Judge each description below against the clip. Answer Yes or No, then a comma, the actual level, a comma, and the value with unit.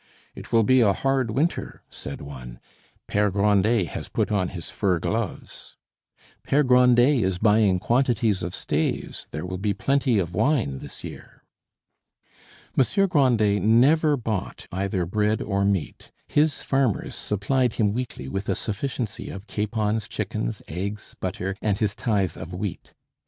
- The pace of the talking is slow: No, average, 145 wpm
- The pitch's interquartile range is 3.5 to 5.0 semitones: Yes, average, 4.7 semitones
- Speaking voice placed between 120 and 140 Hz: No, low, 105 Hz